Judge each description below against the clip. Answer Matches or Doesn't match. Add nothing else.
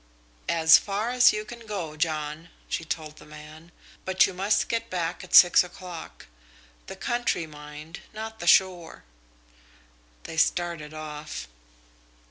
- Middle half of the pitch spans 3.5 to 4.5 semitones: Matches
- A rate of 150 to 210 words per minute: Doesn't match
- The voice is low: Doesn't match